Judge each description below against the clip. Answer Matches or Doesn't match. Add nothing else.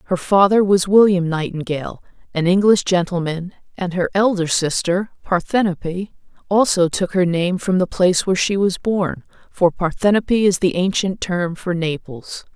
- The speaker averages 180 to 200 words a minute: Doesn't match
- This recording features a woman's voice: Matches